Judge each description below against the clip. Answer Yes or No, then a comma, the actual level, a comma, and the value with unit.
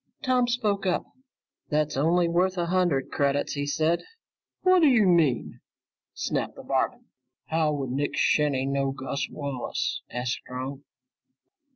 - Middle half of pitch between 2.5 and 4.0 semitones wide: No, average, 4.8 semitones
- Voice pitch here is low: No, medium, 150 Hz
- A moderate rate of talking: No, slow, 130 wpm